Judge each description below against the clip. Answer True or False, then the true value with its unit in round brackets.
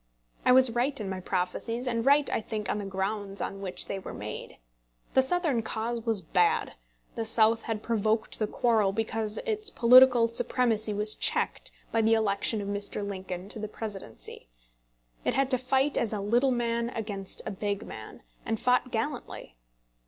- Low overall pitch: False (225 Hz)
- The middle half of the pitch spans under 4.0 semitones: True (3.3 semitones)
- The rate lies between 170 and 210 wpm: True (175 wpm)